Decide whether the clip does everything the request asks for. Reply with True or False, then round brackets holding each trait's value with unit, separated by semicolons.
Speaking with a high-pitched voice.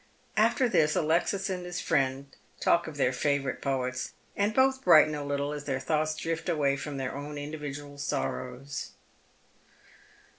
False (145 Hz)